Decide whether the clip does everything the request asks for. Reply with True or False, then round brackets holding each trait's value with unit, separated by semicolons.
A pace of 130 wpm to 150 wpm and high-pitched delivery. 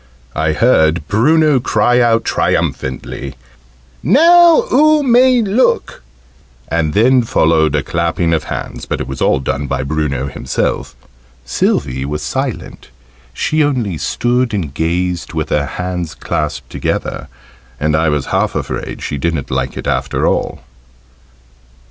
False (135 wpm; 85 Hz)